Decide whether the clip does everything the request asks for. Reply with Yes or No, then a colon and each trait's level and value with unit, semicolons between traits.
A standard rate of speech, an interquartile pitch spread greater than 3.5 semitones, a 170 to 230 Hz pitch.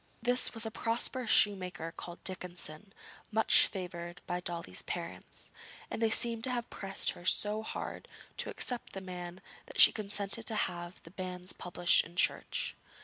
Yes: average, 160 wpm; average, 4.0 semitones; high, 190 Hz